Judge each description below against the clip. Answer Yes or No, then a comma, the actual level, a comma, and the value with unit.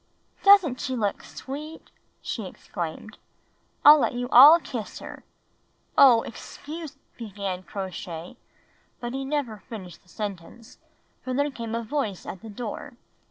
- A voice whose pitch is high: Yes, high, 240 Hz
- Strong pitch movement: Yes, wide, 5.8 semitones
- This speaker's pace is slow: No, average, 150 wpm